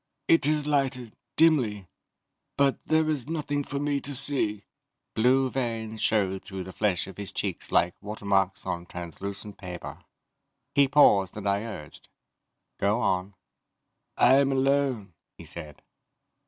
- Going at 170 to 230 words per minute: No, average, 140 wpm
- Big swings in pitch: Yes, wide, 6.2 semitones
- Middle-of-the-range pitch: No, low, 110 Hz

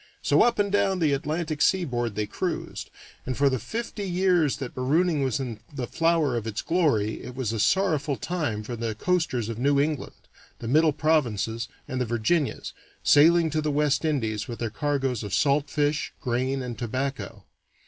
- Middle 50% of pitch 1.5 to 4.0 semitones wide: No, average, 5.0 semitones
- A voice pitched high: No, medium, 140 Hz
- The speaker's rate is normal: Yes, average, 180 wpm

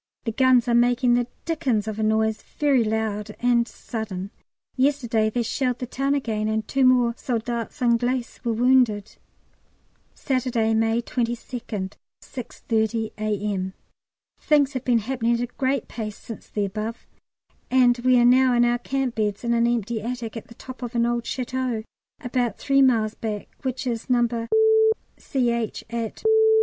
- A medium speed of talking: Yes, average, 160 wpm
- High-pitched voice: Yes, high, 235 Hz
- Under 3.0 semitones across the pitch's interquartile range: Yes, narrow, 2.4 semitones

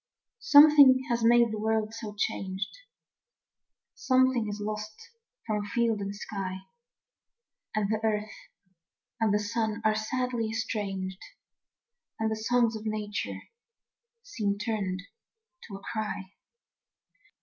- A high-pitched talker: Yes, high, 215 Hz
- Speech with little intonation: Yes, narrow, 1.9 semitones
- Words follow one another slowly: Yes, slow, 110 wpm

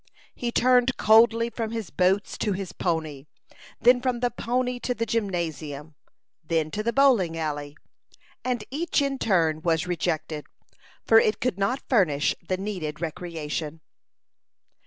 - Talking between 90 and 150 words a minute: Yes, average, 140 wpm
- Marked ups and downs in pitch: Yes, wide, 6.8 semitones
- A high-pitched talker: Yes, high, 195 Hz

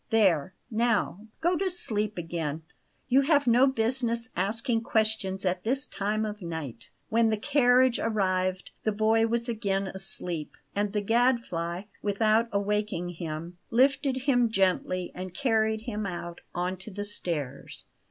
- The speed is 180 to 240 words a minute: No, average, 145 wpm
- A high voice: Yes, high, 215 Hz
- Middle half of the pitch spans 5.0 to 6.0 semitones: No, average, 4.1 semitones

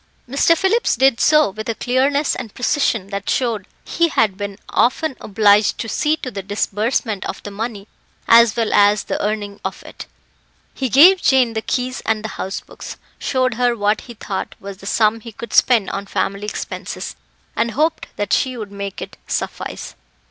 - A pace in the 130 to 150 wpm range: No, average, 185 wpm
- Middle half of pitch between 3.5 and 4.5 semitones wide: Yes, average, 4.0 semitones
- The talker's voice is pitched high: Yes, high, 225 Hz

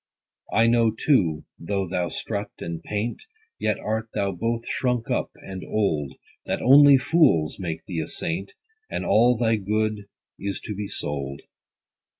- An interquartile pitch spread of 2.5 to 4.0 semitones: No, average, 4.8 semitones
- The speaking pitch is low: Yes, low, 105 Hz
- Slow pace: No, average, 155 wpm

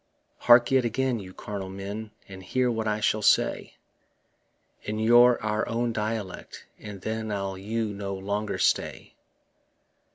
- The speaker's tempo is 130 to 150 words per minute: Yes, slow, 135 wpm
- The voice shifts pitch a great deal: No, narrow, 2.6 semitones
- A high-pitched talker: No, low, 110 Hz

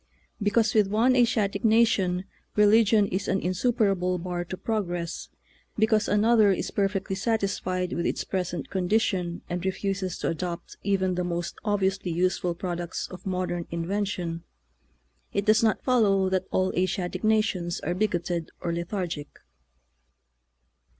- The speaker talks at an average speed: No, slow, 130 wpm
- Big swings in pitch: No, average, 2.9 semitones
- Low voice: No, high, 190 Hz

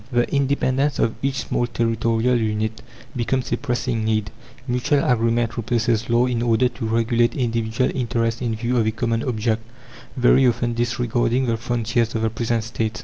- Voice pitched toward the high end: No, low, 115 Hz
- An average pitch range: No, narrow, 1.5 semitones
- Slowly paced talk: No, average, 165 wpm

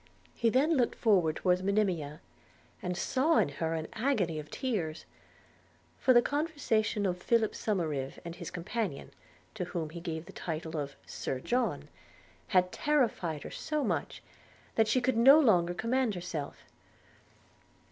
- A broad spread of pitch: Yes, wide, 6.6 semitones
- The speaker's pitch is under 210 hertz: Yes, high, 190 Hz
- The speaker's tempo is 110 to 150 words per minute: Yes, average, 145 wpm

